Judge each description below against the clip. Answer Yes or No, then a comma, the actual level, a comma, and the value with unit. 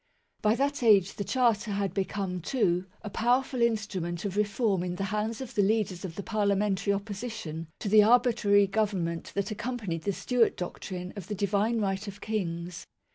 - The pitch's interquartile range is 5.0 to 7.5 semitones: No, average, 2.7 semitones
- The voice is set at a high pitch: Yes, high, 205 Hz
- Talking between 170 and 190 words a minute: Yes, average, 180 wpm